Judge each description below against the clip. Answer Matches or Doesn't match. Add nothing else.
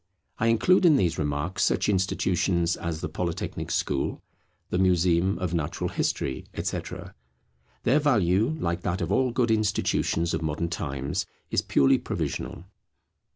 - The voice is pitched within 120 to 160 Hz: Doesn't match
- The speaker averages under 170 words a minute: Matches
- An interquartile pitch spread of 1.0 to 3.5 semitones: Doesn't match